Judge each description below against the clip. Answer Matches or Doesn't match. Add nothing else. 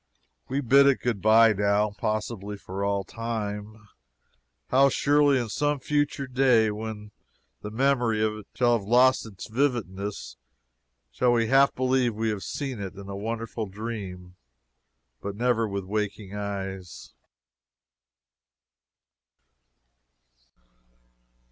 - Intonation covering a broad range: Doesn't match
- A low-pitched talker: Matches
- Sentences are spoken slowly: Matches